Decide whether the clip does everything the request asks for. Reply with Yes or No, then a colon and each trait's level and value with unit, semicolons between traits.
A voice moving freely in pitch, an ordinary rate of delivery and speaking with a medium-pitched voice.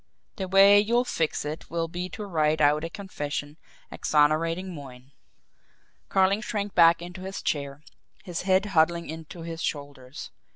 No: average, 4.0 semitones; average, 150 wpm; medium, 165 Hz